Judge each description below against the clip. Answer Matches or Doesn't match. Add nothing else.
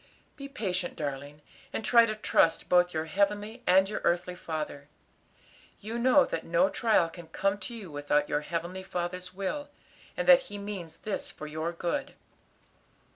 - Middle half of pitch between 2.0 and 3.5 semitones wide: Doesn't match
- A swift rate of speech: Doesn't match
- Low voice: Doesn't match